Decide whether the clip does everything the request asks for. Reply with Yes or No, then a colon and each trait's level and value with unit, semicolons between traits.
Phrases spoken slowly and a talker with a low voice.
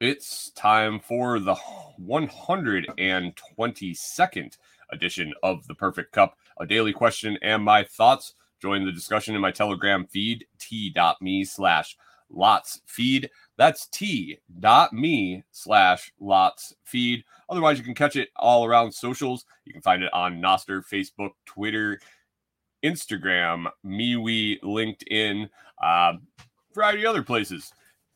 Yes: slow, 125 wpm; low, 110 Hz